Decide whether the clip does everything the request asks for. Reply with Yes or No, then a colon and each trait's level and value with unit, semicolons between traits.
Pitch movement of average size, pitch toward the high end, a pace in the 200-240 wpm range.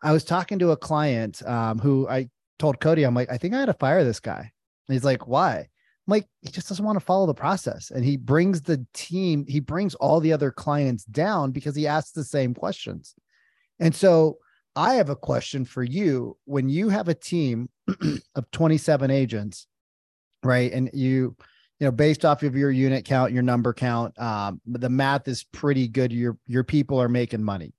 No: average, 4.1 semitones; low, 135 Hz; fast, 205 wpm